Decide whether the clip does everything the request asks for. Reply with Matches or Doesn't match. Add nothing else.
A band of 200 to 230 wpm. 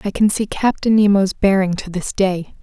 Matches